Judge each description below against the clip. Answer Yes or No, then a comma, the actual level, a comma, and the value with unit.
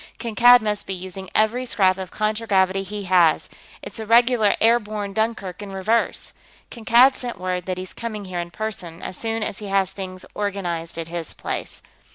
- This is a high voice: Yes, high, 200 Hz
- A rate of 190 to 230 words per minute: No, average, 180 wpm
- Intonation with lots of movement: No, average, 3.2 semitones